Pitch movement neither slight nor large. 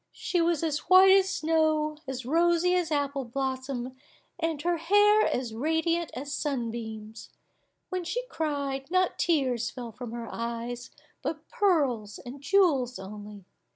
No: wide, 5.8 semitones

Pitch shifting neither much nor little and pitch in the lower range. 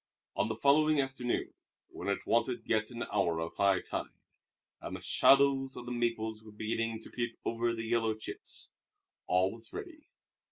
No: narrow, 2.3 semitones; low, 115 Hz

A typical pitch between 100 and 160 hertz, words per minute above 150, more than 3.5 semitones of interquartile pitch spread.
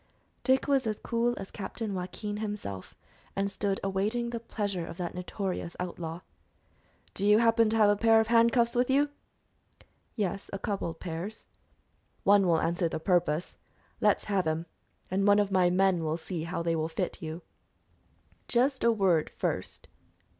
No: high, 195 Hz; average, 170 wpm; average, 4.3 semitones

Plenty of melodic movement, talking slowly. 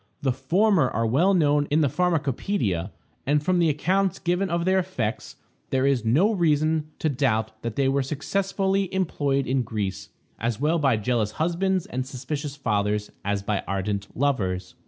No: wide, 7.0 semitones; average, 165 wpm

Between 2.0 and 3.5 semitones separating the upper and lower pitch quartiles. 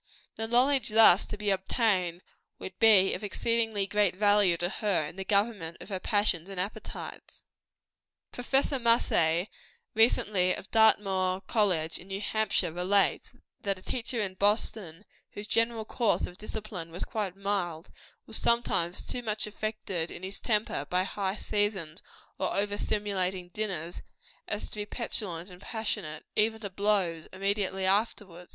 Yes: average, 2.9 semitones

